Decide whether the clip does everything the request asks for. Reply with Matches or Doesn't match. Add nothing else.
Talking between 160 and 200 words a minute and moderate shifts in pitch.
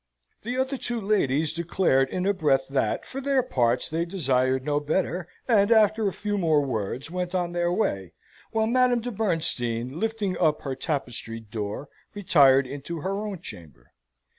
Doesn't match